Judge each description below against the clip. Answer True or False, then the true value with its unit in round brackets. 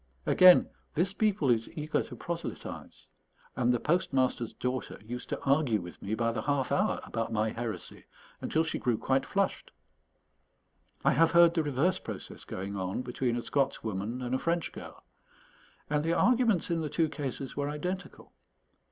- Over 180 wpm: False (170 wpm)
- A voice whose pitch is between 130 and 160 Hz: True (140 Hz)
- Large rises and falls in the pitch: True (5.8 semitones)